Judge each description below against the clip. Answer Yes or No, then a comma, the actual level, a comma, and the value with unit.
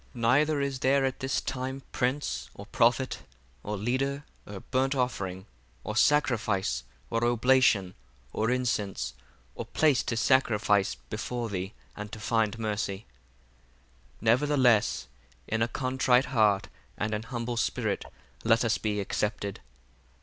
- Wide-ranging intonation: No, average, 3.9 semitones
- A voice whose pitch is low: Yes, low, 115 Hz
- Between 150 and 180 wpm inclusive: No, slow, 135 wpm